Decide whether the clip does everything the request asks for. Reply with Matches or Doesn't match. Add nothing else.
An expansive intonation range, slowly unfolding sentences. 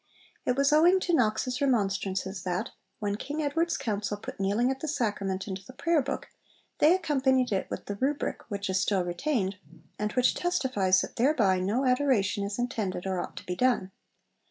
Doesn't match